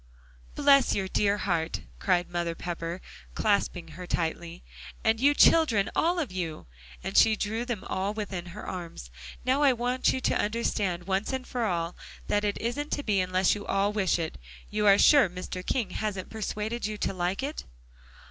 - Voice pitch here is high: Yes, high, 200 Hz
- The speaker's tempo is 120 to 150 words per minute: No, average, 175 wpm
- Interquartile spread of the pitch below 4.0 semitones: No, average, 4.4 semitones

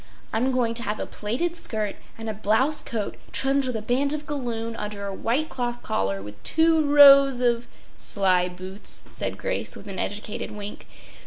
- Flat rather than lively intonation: No, average, 4.9 semitones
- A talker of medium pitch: No, high, 230 Hz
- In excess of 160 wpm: Yes, average, 180 wpm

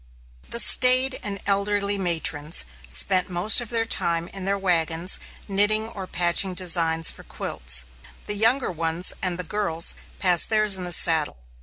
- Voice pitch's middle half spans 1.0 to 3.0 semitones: No, average, 3.7 semitones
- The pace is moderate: Yes, average, 155 wpm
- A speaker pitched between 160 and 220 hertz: Yes, medium, 185 Hz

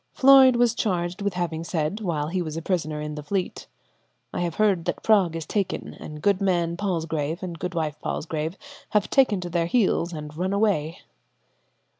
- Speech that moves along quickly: No, average, 175 wpm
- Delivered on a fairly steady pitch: No, average, 4.0 semitones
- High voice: No, medium, 175 Hz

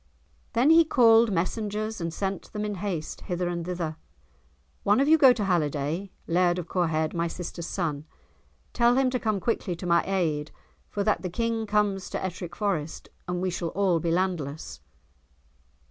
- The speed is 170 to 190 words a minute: Yes, average, 175 wpm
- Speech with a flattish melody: No, average, 3.9 semitones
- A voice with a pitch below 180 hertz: No, medium, 185 Hz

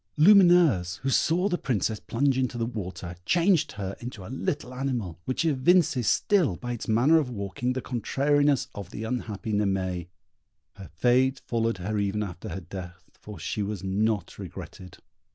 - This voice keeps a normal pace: Yes, average, 160 wpm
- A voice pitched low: Yes, low, 115 Hz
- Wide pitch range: Yes, wide, 5.7 semitones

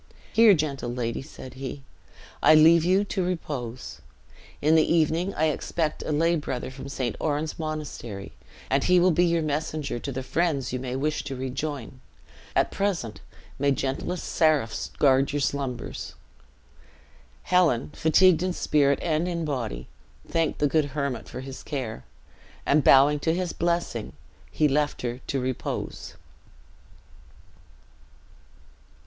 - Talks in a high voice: No, medium, 145 Hz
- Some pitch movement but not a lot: Yes, average, 3.8 semitones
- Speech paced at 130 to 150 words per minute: Yes, average, 140 wpm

